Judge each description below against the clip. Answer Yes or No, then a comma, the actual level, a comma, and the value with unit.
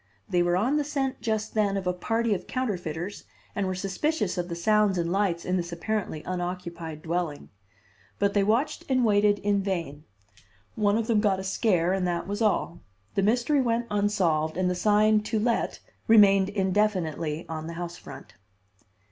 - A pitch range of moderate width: Yes, average, 3.5 semitones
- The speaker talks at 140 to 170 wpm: No, average, 180 wpm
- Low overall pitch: No, high, 195 Hz